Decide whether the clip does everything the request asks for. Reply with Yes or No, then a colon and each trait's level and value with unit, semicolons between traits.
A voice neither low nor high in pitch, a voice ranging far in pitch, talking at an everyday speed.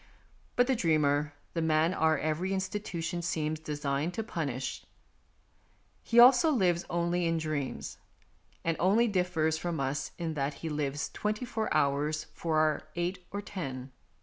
No: medium, 165 Hz; average, 3.5 semitones; average, 150 wpm